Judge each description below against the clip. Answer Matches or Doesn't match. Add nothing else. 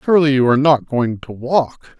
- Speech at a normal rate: Doesn't match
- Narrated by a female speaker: Doesn't match